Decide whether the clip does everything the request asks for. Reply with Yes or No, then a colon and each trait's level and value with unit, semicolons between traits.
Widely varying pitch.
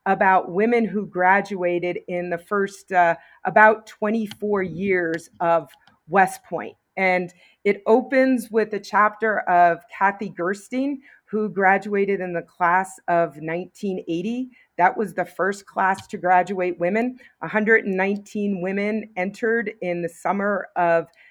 No: average, 3.1 semitones